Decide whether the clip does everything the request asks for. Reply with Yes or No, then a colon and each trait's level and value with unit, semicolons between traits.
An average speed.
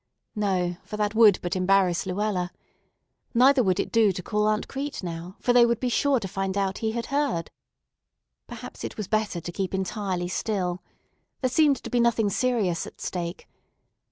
Yes: average, 185 wpm